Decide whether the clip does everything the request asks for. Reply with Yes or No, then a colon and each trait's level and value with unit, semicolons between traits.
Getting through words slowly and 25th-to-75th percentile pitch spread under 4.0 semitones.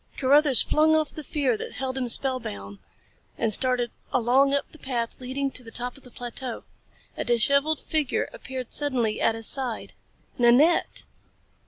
No: average, 160 wpm; average, 2.8 semitones